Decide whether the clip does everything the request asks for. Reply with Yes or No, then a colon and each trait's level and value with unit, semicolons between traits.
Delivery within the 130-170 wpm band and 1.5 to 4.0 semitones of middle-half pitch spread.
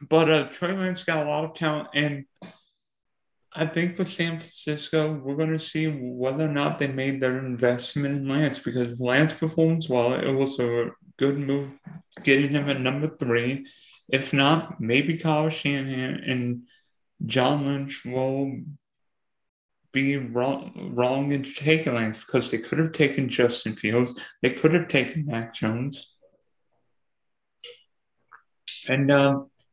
Yes: average, 145 wpm; average, 3.3 semitones